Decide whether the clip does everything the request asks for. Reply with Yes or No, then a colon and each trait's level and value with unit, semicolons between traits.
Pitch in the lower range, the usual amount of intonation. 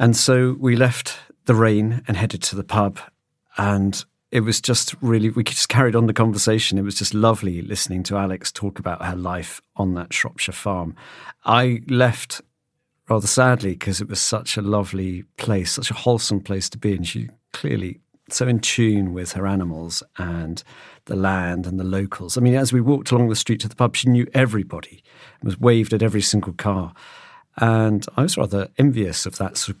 Yes: low, 105 Hz; average, 3.8 semitones